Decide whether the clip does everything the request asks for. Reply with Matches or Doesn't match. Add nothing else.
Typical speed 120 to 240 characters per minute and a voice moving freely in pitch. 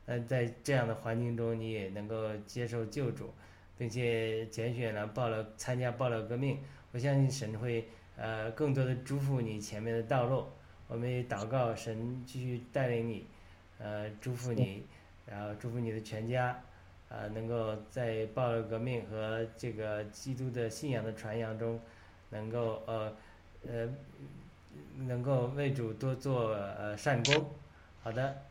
Doesn't match